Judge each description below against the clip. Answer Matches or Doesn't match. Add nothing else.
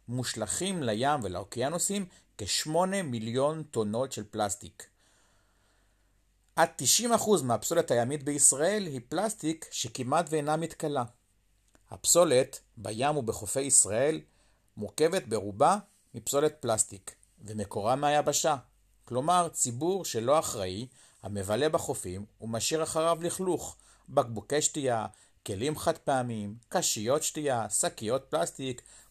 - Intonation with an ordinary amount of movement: Doesn't match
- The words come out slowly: Matches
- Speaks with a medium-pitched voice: Doesn't match